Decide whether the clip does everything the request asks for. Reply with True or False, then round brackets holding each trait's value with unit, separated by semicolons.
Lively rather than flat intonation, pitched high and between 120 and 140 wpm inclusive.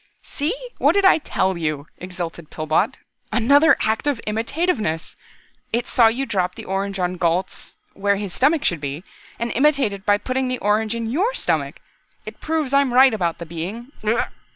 False (6.8 semitones; 220 Hz; 175 wpm)